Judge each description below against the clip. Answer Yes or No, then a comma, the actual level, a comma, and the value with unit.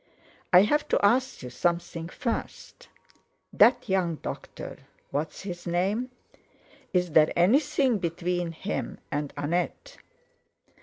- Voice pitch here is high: No, medium, 180 Hz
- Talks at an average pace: No, slow, 105 wpm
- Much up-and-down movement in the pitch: No, average, 4.2 semitones